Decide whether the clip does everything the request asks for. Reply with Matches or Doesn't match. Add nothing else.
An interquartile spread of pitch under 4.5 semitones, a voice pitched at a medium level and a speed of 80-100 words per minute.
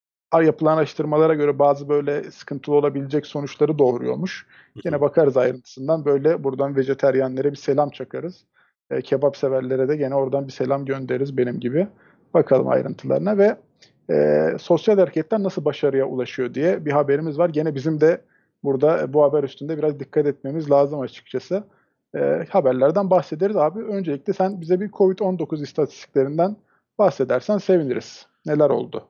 Doesn't match